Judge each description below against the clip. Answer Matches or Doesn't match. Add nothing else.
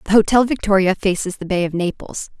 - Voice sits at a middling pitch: Doesn't match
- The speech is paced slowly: Doesn't match